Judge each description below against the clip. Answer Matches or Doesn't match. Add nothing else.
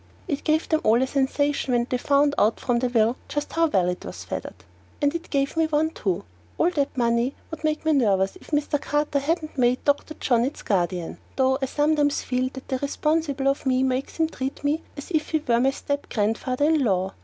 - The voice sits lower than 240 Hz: Doesn't match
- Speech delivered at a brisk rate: Matches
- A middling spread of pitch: Matches